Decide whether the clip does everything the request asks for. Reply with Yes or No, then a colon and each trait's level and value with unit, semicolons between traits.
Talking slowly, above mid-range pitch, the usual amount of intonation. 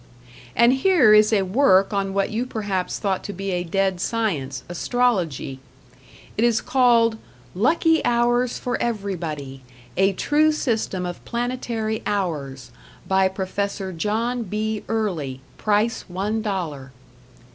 Yes: slow, 125 wpm; high, 205 Hz; average, 4.2 semitones